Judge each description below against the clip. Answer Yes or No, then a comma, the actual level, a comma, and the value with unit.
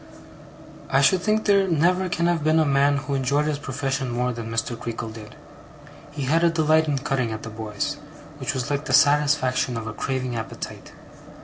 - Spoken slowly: No, average, 195 wpm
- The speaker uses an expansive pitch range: No, average, 3.9 semitones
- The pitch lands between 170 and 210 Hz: No, medium, 140 Hz